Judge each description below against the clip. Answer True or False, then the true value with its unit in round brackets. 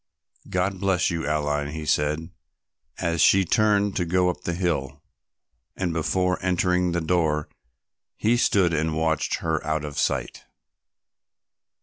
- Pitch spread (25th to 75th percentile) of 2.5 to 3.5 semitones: True (2.9 semitones)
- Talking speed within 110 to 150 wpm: True (135 wpm)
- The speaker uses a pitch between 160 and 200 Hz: False (85 Hz)